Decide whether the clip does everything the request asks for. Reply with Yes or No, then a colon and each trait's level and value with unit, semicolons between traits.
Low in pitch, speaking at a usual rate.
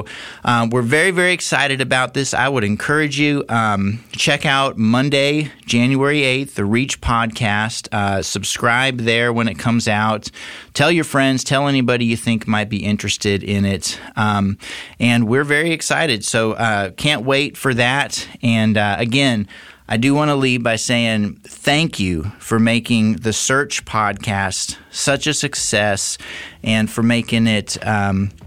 Yes: low, 115 Hz; average, 160 wpm